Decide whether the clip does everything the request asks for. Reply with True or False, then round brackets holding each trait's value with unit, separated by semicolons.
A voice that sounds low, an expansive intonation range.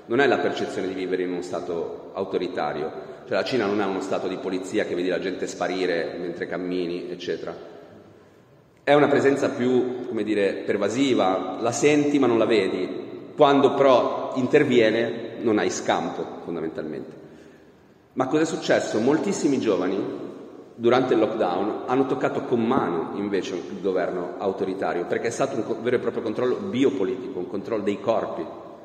True (120 Hz; 7.5 semitones)